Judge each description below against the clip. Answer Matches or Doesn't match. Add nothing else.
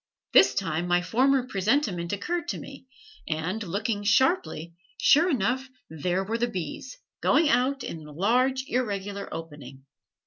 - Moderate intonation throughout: Doesn't match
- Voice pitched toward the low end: Doesn't match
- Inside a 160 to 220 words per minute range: Doesn't match